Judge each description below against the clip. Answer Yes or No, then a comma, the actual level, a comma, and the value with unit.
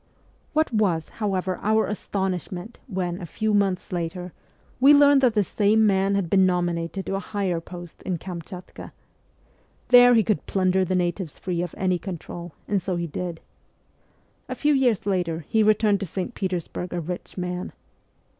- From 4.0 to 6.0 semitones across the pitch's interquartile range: No, average, 2.9 semitones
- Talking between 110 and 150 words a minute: No, average, 165 wpm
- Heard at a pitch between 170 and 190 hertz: Yes, medium, 185 Hz